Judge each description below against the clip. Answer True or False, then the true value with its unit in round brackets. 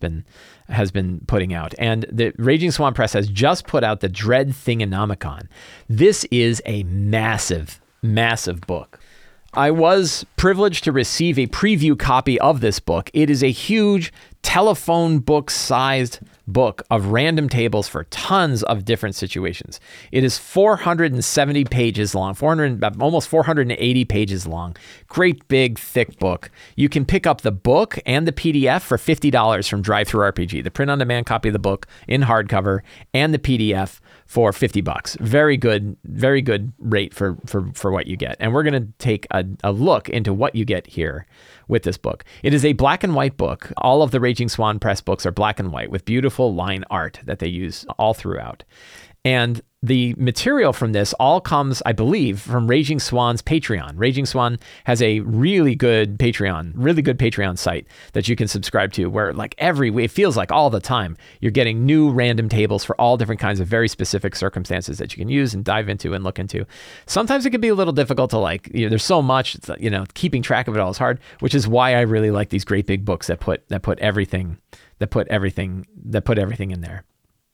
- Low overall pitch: True (115 Hz)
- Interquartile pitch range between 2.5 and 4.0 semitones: False (5.3 semitones)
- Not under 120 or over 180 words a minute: False (195 wpm)